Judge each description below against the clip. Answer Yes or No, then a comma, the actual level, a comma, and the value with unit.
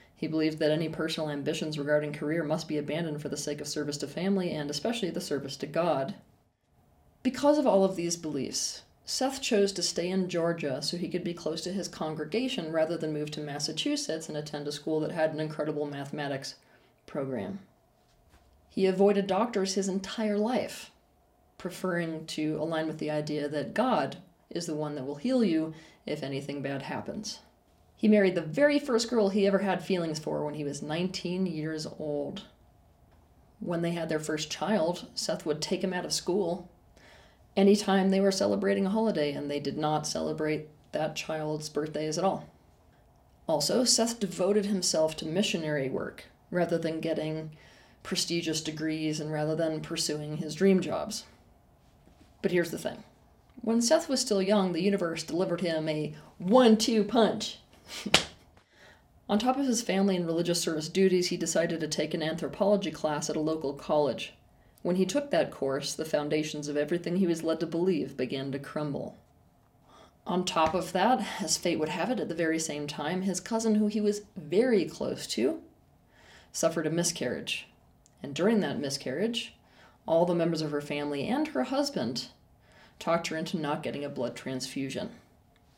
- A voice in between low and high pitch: Yes, medium, 165 Hz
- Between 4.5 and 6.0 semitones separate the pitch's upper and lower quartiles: No, average, 4.1 semitones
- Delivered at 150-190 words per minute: Yes, average, 175 wpm